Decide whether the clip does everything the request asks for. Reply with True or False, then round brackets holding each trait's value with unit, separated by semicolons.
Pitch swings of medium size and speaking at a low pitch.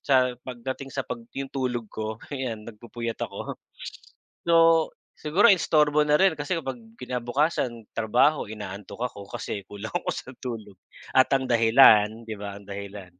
True (4.1 semitones; 120 Hz)